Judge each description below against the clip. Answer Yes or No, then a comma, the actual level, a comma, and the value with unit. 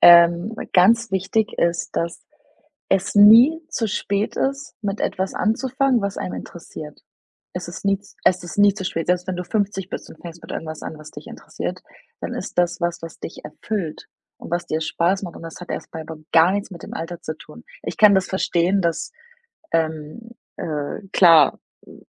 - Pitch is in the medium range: Yes, medium, 180 Hz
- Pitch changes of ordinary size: Yes, average, 3.4 semitones